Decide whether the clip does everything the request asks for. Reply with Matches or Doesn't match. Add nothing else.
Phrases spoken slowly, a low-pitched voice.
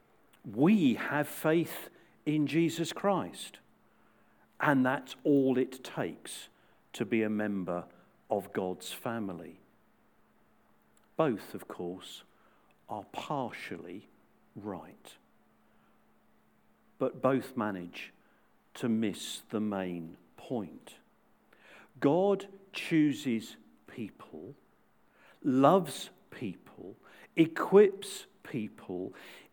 Matches